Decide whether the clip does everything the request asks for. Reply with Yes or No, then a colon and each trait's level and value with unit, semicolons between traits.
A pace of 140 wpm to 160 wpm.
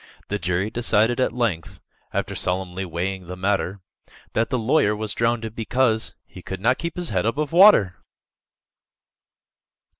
Yes: average, 145 wpm